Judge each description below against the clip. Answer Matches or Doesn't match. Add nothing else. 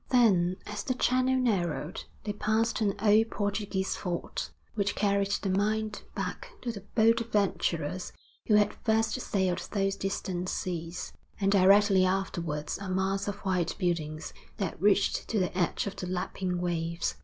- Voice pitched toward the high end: Matches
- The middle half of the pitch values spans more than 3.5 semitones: Doesn't match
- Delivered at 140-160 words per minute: Matches